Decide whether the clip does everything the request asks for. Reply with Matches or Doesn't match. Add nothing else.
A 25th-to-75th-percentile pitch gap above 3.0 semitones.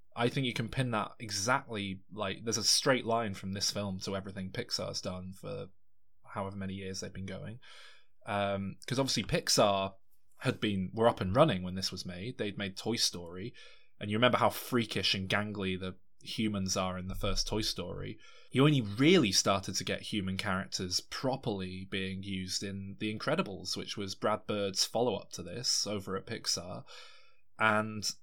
Doesn't match